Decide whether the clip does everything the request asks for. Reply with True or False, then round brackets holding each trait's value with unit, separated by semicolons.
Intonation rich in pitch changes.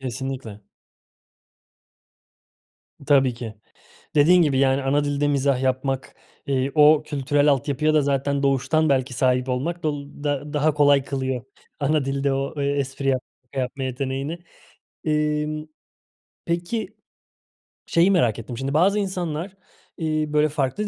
False (2.4 semitones)